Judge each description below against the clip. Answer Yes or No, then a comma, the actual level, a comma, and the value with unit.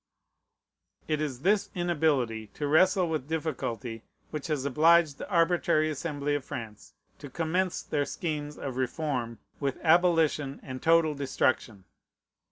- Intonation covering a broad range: No, average, 3.6 semitones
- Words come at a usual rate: No, slow, 130 wpm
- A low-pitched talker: No, medium, 150 Hz